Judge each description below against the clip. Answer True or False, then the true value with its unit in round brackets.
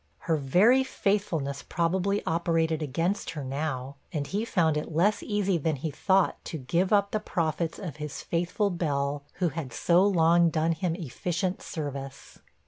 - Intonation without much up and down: False (3.9 semitones)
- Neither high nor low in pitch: True (165 Hz)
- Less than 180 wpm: True (160 wpm)